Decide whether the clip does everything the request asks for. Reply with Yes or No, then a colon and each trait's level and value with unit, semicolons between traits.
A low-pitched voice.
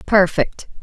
No: high, 190 Hz